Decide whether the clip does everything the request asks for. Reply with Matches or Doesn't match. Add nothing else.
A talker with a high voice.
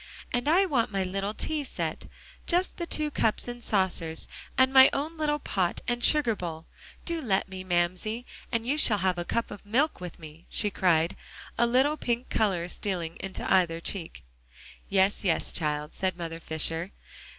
Matches